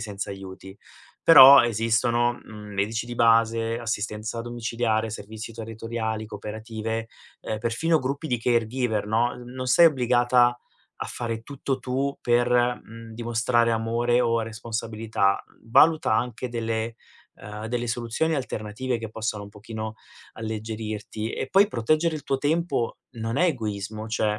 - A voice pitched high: No, low, 115 Hz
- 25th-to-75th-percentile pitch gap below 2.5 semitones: Yes, narrow, 1.8 semitones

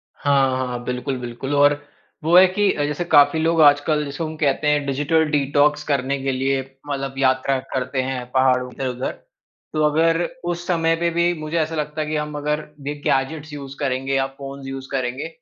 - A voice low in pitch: No, medium, 145 Hz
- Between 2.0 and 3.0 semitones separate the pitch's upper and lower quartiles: Yes, narrow, 2.5 semitones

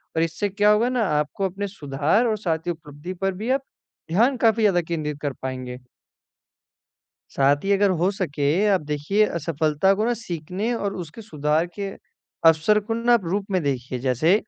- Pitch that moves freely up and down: Yes, wide, 5.7 semitones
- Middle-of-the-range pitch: Yes, medium, 180 Hz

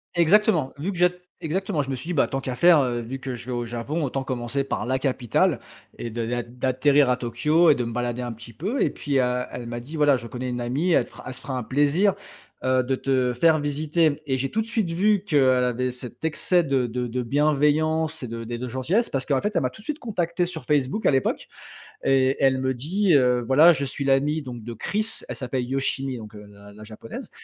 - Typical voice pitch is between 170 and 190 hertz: No, low, 135 Hz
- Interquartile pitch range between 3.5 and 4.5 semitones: Yes, average, 4.2 semitones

